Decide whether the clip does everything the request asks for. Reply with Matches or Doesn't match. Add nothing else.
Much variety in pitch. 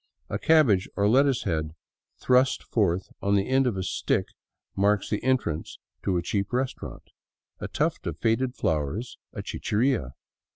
Matches